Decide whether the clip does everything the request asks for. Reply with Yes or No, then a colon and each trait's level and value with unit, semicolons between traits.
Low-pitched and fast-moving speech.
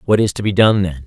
Yes: low, 100 Hz; fast, 335 wpm